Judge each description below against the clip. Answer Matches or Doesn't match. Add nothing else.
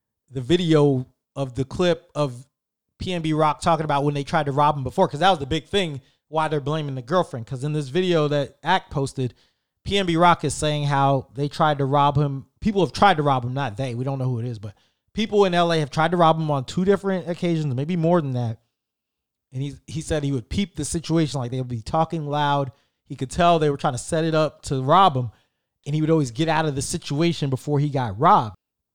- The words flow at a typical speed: Doesn't match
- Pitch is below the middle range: Doesn't match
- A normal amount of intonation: Matches